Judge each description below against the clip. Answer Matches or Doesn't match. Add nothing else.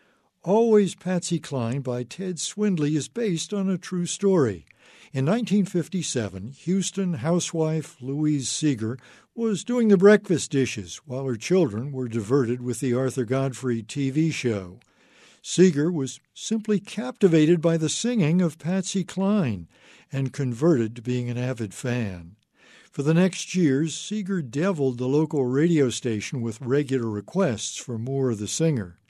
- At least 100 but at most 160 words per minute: Matches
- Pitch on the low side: Doesn't match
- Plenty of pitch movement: Matches